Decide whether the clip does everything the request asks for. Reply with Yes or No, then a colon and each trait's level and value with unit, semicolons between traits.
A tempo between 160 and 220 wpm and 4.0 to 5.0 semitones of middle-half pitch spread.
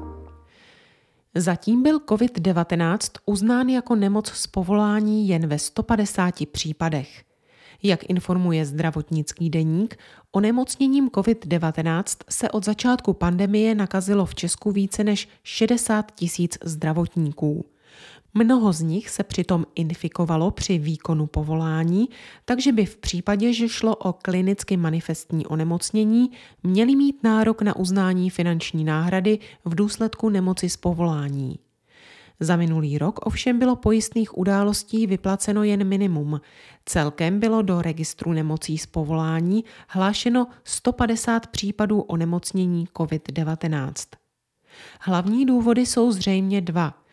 No: slow, 115 wpm; average, 4.7 semitones